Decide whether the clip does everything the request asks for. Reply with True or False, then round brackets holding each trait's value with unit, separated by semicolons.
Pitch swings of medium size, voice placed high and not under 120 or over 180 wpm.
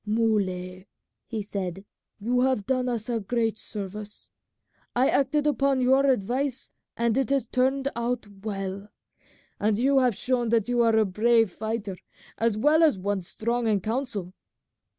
True (3.8 semitones; 230 Hz; 150 wpm)